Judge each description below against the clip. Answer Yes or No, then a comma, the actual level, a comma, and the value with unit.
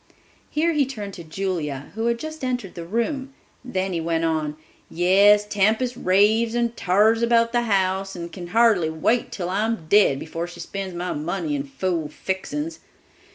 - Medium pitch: No, high, 195 Hz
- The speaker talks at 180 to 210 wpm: No, average, 170 wpm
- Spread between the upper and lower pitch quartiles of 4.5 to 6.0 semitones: Yes, average, 5.2 semitones